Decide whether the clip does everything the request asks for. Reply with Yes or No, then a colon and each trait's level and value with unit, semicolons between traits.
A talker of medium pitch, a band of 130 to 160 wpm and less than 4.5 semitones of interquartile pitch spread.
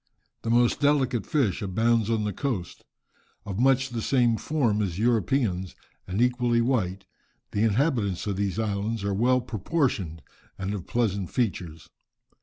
No: low, 110 Hz; average, 145 wpm; average, 3.8 semitones